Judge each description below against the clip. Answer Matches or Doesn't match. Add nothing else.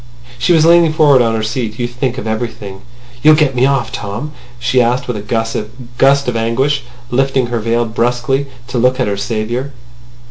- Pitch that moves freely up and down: Doesn't match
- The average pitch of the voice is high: Doesn't match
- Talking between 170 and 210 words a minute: Matches